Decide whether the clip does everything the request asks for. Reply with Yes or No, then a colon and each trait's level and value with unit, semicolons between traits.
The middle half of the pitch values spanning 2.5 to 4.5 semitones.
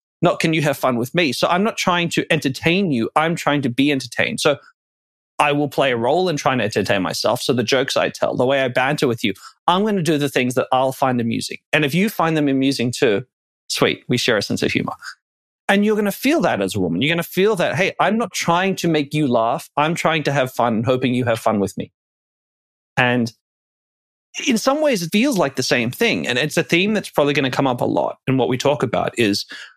No: wide, 5.6 semitones